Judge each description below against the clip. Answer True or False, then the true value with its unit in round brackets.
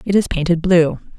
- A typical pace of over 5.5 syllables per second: False (5.3 syllables/s)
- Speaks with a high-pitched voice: False (175 Hz)